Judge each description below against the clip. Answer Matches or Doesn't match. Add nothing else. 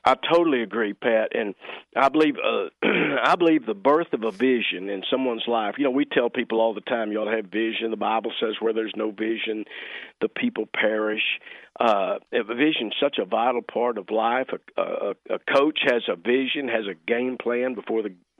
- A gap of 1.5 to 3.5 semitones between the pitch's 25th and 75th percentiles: Matches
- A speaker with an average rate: Doesn't match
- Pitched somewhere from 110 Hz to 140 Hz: Matches